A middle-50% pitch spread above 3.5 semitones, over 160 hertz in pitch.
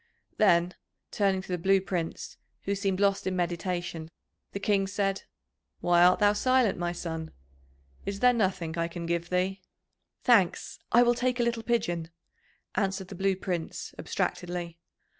No: narrow, 2.6 semitones; high, 190 Hz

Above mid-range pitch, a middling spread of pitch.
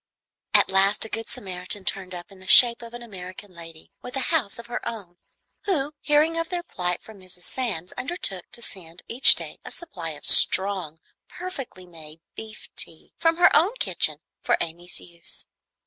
No: high, 200 Hz; wide, 6.3 semitones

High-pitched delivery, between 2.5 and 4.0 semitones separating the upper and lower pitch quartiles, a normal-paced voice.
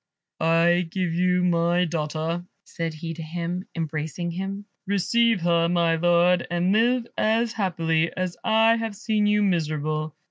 No: medium, 175 Hz; average, 3.1 semitones; average, 145 wpm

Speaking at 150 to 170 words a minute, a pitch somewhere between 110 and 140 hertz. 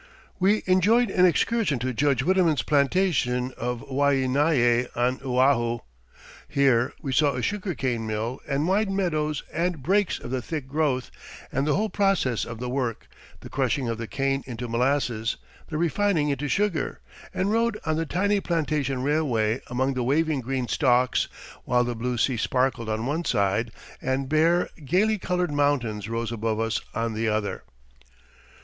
Yes: average, 160 wpm; low, 135 Hz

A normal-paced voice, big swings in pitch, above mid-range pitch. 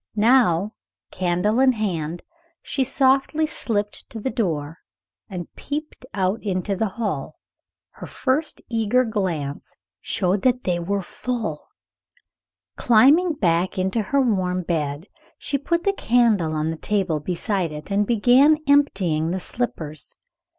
No: slow, 130 wpm; wide, 6.3 semitones; high, 205 Hz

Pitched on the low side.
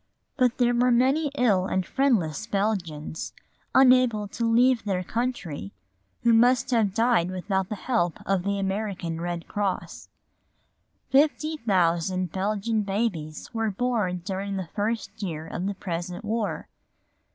No: high, 205 Hz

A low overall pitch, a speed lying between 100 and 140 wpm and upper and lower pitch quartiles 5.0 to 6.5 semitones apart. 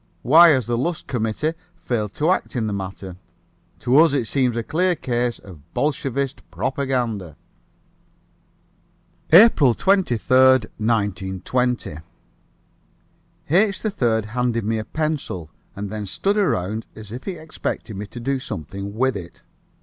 Yes: low, 120 Hz; slow, 135 wpm; wide, 5.4 semitones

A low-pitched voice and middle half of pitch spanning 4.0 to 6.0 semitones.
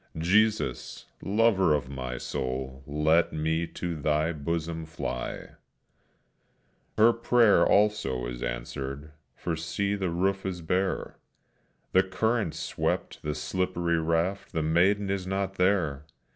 Yes: very low, 85 Hz; average, 4.4 semitones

